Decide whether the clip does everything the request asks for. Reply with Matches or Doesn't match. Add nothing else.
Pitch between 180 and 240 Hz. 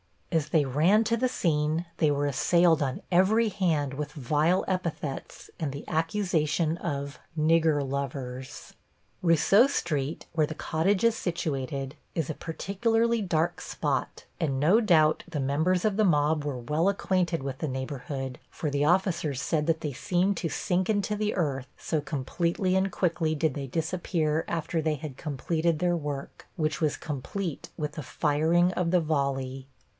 Doesn't match